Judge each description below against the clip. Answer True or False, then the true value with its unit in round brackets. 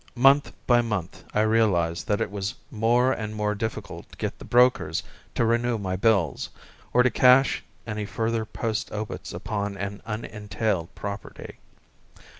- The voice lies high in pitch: False (110 Hz)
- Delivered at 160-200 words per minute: False (150 wpm)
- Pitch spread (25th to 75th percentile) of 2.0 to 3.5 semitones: True (2.5 semitones)